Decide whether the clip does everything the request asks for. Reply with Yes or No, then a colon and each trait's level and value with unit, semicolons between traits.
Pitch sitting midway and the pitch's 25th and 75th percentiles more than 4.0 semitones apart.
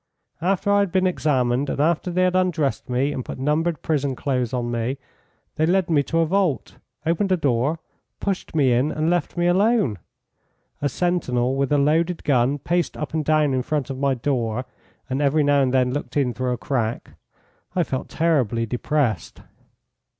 Yes: medium, 145 Hz; average, 4.7 semitones